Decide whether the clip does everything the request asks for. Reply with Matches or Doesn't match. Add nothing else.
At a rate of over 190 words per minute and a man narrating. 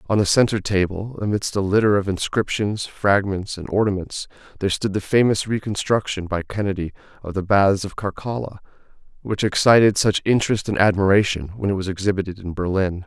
Doesn't match